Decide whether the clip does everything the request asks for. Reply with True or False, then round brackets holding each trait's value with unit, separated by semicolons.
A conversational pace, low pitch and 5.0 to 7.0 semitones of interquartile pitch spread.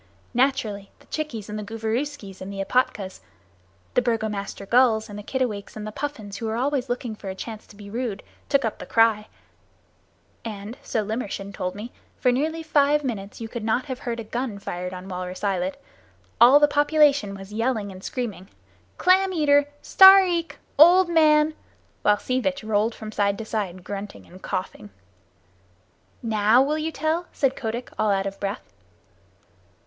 False (170 wpm; 225 Hz; 5.5 semitones)